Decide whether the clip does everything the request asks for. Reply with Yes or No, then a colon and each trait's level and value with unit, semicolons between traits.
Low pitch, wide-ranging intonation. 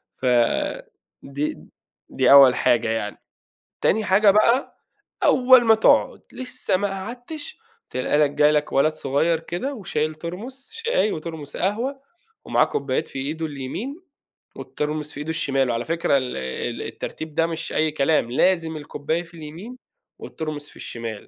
No: medium, 160 Hz; wide, 6.7 semitones